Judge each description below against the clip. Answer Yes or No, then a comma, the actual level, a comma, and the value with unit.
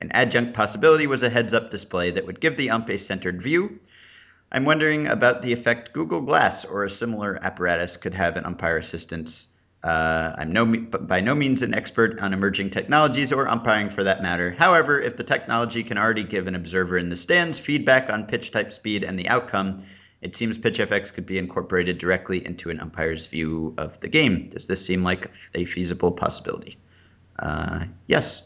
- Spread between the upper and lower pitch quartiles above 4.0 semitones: Yes, average, 4.7 semitones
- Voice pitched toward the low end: Yes, low, 100 Hz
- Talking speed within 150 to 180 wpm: No, average, 190 wpm